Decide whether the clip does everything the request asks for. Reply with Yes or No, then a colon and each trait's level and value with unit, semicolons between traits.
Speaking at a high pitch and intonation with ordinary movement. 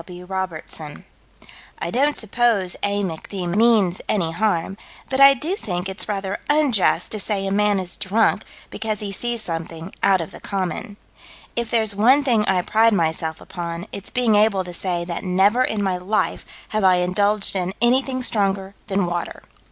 Yes: high, 195 Hz; average, 3.5 semitones